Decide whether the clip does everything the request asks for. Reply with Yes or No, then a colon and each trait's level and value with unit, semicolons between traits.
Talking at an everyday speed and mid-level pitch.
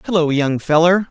Yes: average, 160 wpm; medium, 165 Hz